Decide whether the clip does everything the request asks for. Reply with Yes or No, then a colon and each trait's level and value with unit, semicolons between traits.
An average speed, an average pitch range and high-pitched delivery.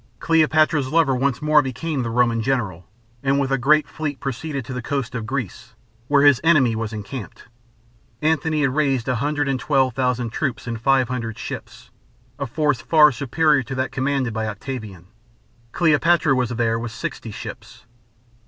No: average, 170 wpm; average, 3.8 semitones; low, 135 Hz